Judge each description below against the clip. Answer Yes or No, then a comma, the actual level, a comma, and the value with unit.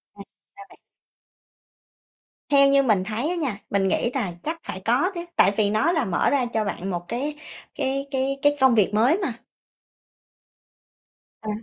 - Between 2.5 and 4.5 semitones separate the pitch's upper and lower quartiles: No, wide, 5.4 semitones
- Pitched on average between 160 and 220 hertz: No, very high, 260 Hz